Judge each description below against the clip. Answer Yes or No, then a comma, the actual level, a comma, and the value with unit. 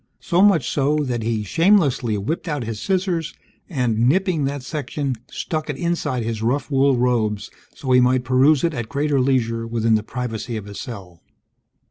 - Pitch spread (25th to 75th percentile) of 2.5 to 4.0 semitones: No, average, 4.7 semitones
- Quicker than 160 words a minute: Yes, average, 175 wpm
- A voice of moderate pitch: No, low, 130 Hz